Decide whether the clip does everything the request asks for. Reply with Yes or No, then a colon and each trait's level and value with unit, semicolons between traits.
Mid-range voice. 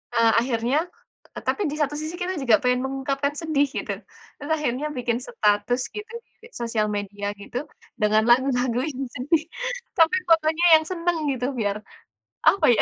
No: very high, 265 Hz